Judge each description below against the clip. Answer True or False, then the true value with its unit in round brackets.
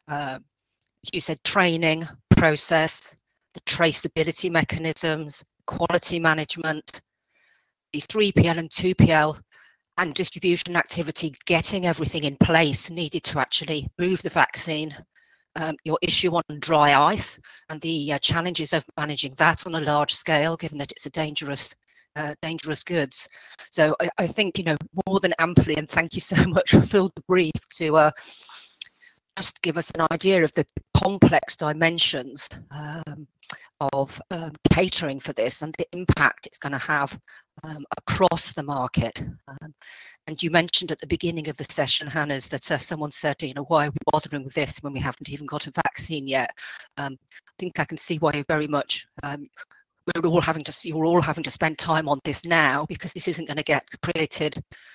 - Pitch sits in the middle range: True (160 Hz)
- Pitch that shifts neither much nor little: False (2.3 semitones)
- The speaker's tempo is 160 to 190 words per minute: True (175 wpm)